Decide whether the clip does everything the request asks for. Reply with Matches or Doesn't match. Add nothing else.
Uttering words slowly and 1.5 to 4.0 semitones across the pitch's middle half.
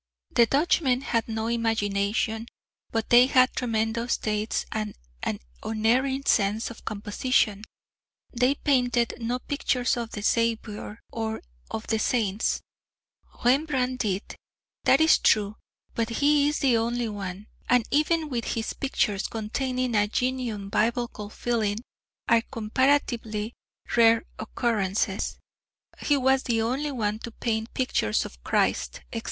Matches